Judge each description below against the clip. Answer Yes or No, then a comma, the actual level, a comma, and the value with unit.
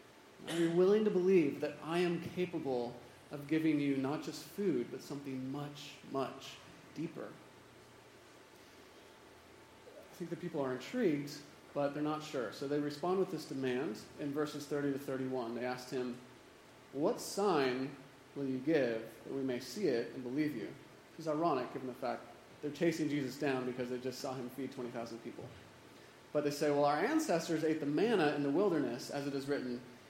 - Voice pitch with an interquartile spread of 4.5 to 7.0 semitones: No, average, 2.9 semitones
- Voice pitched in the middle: Yes, medium, 145 Hz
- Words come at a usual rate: Yes, average, 180 wpm